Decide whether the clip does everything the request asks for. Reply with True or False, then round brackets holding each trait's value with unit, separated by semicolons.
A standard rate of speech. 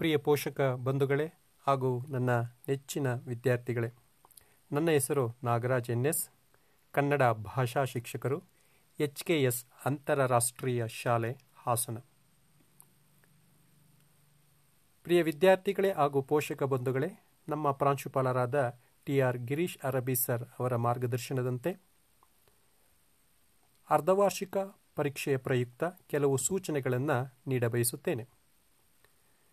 True (80 wpm)